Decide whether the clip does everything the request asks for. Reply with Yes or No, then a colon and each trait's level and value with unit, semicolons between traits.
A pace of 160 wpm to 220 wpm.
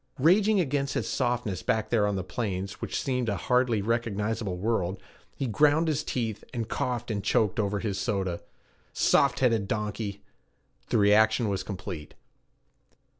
No: average, 150 wpm